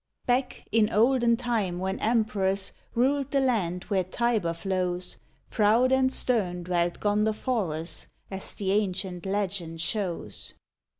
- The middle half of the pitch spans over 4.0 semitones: Yes, average, 4.6 semitones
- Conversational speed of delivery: No, slow, 120 wpm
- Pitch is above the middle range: Yes, high, 205 Hz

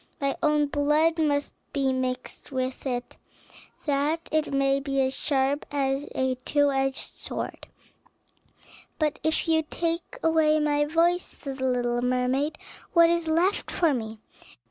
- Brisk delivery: No, average, 145 wpm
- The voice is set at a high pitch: Yes, very high, 285 Hz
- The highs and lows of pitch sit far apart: No, average, 2.9 semitones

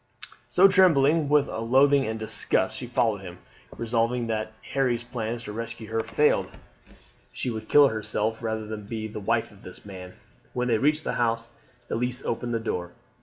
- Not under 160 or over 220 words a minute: Yes, average, 180 wpm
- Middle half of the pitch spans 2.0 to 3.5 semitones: Yes, average, 2.8 semitones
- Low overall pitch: Yes, low, 115 Hz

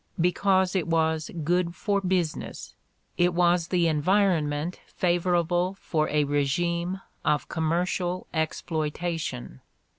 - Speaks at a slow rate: Yes, slow, 100 wpm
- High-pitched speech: No, medium, 170 Hz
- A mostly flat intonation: Yes, narrow, 2.3 semitones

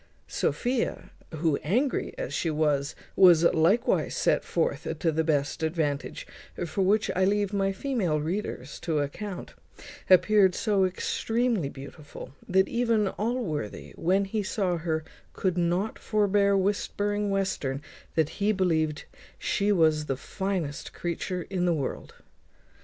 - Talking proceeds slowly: Yes, slow, 130 wpm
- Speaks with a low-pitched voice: No, medium, 185 Hz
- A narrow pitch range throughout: No, average, 4.5 semitones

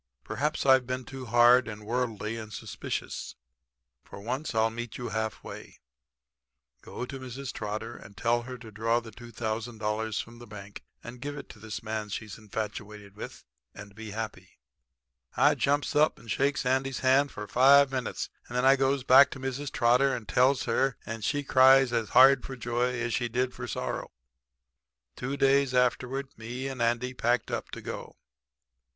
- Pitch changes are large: No, average, 3.1 semitones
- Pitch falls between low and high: No, low, 120 Hz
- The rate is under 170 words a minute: No, average, 175 wpm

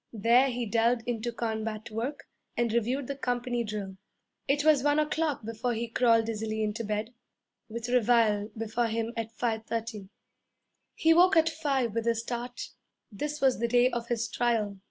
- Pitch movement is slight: Yes, narrow, 2.1 semitones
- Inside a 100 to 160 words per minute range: No, average, 170 wpm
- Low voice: No, high, 235 Hz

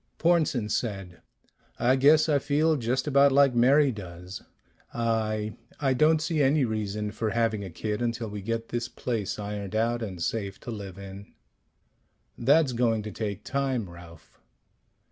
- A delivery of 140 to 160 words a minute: Yes, average, 155 wpm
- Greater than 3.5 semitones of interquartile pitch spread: Yes, average, 4.6 semitones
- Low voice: Yes, low, 115 Hz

